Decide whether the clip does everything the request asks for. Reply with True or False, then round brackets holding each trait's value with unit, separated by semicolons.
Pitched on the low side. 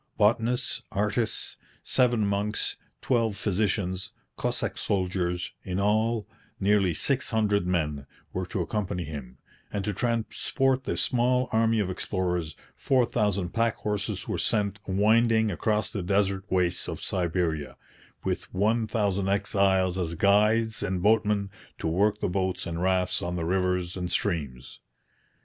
True (100 Hz)